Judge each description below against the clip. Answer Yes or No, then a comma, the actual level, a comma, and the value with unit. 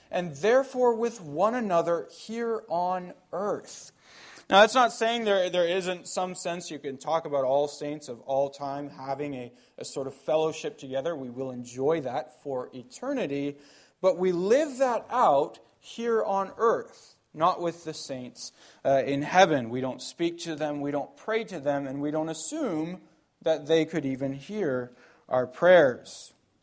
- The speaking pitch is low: No, medium, 160 Hz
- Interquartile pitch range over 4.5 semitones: Yes, wide, 5.4 semitones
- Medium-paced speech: Yes, average, 170 wpm